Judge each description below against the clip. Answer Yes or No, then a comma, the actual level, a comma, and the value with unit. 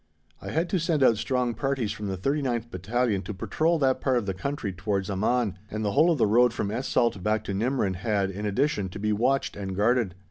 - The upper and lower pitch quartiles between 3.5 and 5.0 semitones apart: Yes, average, 4.7 semitones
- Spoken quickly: Yes, fast, 235 wpm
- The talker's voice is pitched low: Yes, low, 110 Hz